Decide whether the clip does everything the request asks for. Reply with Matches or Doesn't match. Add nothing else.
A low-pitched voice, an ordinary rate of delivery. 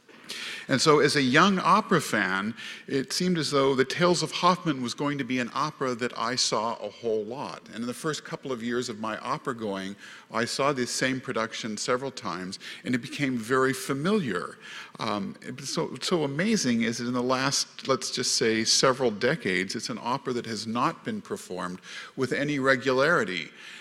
Matches